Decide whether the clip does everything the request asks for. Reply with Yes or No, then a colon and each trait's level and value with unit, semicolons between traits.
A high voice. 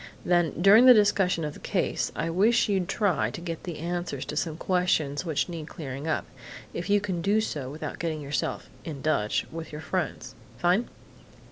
No: medium, 170 Hz